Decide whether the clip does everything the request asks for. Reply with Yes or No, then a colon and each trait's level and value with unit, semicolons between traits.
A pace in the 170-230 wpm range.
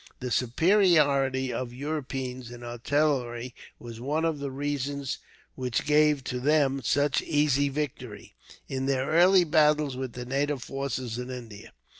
No: average, 140 wpm